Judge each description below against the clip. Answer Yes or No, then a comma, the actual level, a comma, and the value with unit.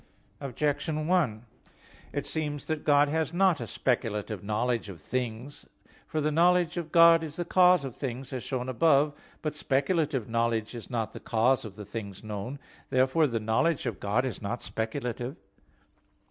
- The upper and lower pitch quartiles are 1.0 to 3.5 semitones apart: No, average, 5.3 semitones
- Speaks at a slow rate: No, average, 175 wpm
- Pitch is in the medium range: No, low, 130 Hz